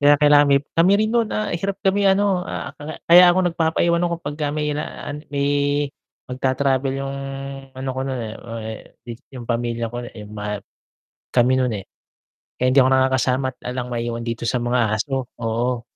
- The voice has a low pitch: Yes, low, 130 Hz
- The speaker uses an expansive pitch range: No, average, 4.0 semitones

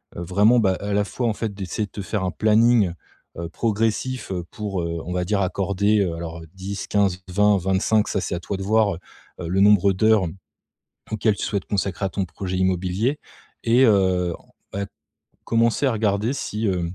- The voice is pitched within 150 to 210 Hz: No, low, 100 Hz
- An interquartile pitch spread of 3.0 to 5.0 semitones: No, narrow, 2.6 semitones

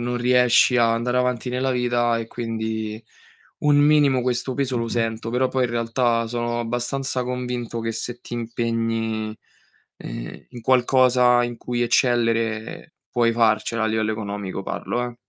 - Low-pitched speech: Yes, low, 120 Hz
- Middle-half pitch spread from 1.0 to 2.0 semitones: Yes, narrow, 1.5 semitones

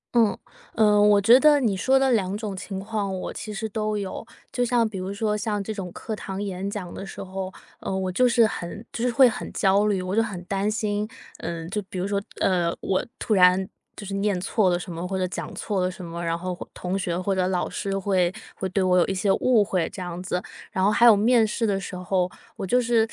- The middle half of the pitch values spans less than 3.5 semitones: Yes, average, 2.7 semitones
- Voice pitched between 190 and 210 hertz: Yes, high, 195 Hz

